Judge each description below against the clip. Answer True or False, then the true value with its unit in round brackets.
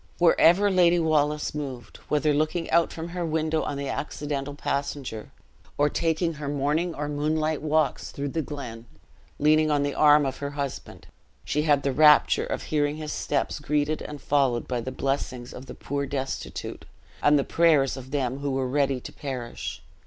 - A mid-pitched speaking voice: True (145 Hz)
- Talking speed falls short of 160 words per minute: False (175 wpm)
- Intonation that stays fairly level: True (2.2 semitones)